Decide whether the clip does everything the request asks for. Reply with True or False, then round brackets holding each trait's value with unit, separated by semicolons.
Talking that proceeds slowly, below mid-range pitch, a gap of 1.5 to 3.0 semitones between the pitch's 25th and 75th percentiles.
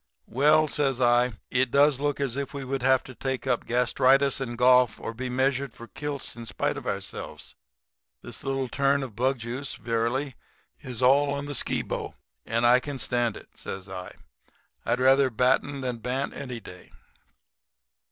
False (170 wpm; 130 Hz; 2.4 semitones)